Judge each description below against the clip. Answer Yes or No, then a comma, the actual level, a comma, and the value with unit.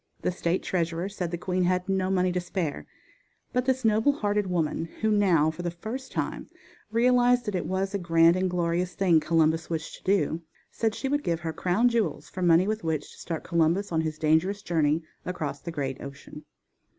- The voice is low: No, medium, 180 Hz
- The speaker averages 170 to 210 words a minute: Yes, average, 200 wpm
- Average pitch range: Yes, average, 3.7 semitones